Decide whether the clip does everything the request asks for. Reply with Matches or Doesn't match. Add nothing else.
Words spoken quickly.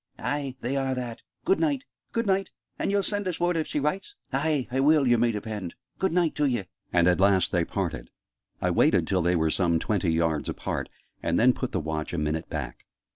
Matches